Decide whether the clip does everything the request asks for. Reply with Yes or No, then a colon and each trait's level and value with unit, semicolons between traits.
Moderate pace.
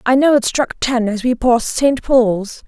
No: fast, 225 wpm